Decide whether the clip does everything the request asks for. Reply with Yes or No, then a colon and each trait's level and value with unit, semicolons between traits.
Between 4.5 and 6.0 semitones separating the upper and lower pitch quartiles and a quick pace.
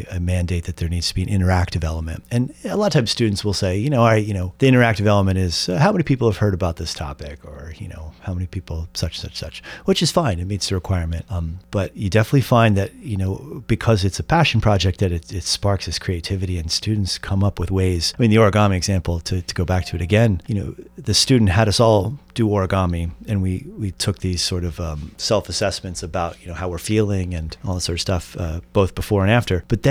No: average, 3.5 semitones; fast, 255 wpm